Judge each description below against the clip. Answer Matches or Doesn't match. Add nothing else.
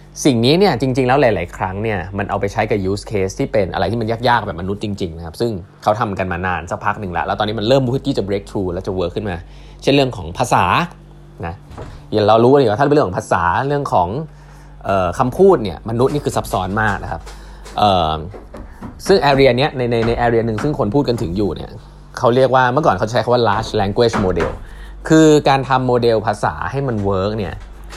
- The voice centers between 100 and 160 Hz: Matches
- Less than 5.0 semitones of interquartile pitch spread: Doesn't match